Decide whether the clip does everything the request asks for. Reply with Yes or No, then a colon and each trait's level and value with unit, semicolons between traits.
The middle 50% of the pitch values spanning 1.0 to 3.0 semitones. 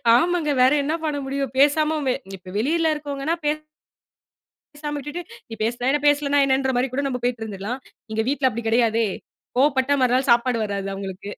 No: average, 3.7 semitones